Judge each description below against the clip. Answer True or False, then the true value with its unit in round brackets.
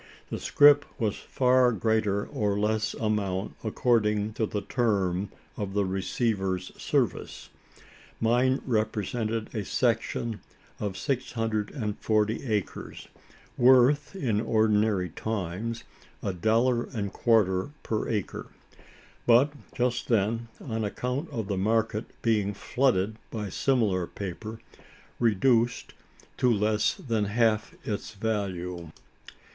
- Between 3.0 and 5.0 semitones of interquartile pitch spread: False (2.5 semitones)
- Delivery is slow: True (115 wpm)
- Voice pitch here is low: True (110 Hz)